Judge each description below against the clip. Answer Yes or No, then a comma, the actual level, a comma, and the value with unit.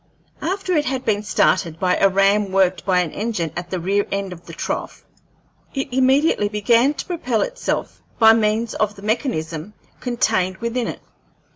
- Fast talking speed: No, average, 170 wpm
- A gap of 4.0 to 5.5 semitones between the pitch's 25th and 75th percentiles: Yes, average, 4.7 semitones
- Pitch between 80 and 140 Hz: No, high, 210 Hz